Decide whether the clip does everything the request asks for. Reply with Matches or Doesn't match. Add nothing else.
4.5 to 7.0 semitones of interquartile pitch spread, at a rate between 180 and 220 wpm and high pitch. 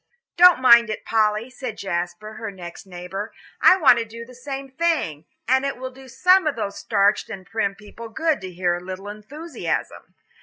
Matches